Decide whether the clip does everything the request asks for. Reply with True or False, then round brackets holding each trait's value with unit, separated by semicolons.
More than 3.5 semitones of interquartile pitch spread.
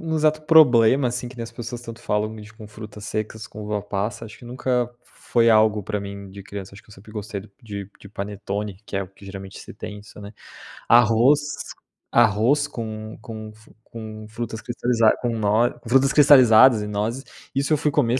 False (2.7 semitones)